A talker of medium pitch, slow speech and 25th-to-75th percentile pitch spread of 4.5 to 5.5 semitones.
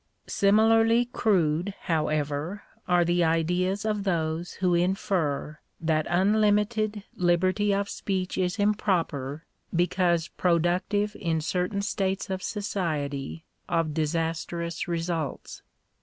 No: medium, 180 Hz; slow, 100 wpm; average, 3.6 semitones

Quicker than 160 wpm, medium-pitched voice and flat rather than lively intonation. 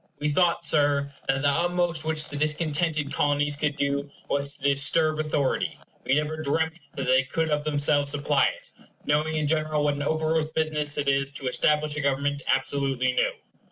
Yes: average, 175 wpm; medium, 145 Hz; narrow, 1.8 semitones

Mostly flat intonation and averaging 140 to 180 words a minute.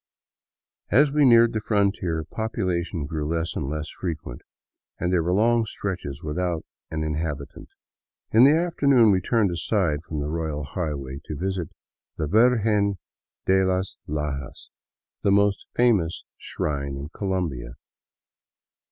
No: wide, 5.4 semitones; average, 150 wpm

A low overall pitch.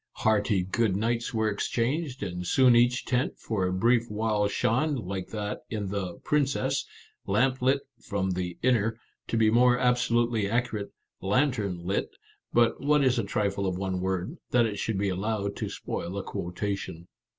Yes: low, 110 Hz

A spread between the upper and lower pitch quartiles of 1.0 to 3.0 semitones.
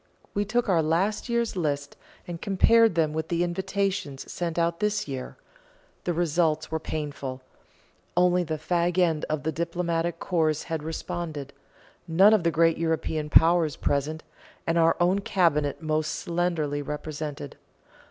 Yes: narrow, 2.4 semitones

